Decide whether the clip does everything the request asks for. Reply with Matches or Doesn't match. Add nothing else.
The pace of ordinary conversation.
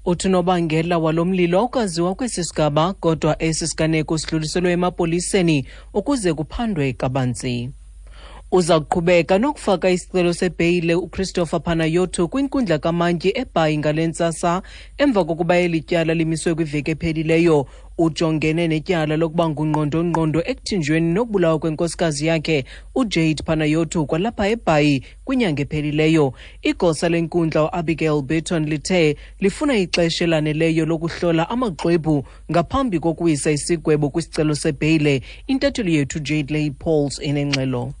Doesn't match